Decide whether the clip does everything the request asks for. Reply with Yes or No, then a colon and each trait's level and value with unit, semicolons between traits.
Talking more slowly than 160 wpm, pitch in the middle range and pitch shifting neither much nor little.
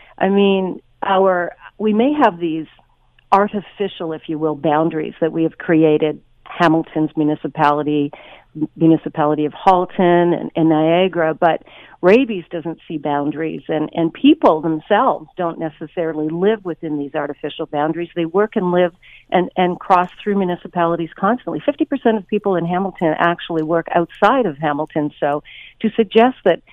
Yes: average, 145 wpm; medium, 170 Hz; average, 3.6 semitones